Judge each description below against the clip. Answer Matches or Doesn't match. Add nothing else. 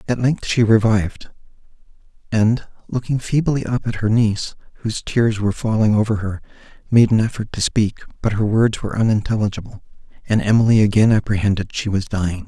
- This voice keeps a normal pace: Matches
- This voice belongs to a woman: Doesn't match